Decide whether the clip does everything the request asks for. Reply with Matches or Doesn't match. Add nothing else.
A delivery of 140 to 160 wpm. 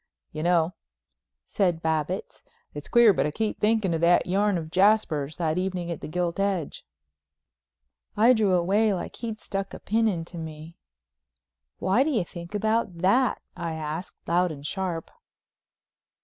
Matches